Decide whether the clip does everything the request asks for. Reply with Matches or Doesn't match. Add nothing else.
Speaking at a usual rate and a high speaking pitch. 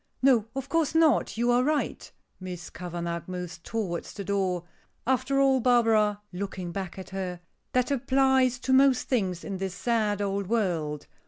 Matches